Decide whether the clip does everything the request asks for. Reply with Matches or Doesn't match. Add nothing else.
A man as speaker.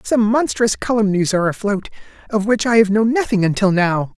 Matches